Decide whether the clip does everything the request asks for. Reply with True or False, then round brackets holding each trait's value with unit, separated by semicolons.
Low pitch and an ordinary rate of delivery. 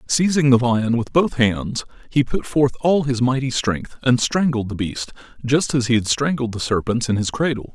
False (125 Hz; 210 wpm)